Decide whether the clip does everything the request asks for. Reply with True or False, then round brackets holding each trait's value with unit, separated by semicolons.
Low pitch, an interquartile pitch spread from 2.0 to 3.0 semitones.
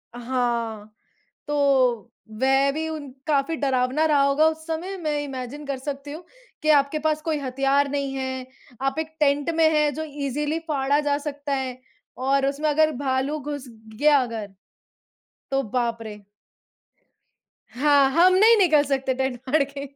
False (280 Hz; 2.4 semitones)